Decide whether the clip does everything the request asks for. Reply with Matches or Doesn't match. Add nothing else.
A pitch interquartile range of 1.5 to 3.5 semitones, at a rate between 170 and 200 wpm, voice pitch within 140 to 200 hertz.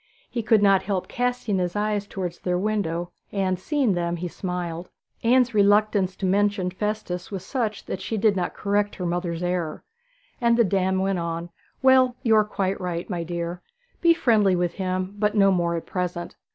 Matches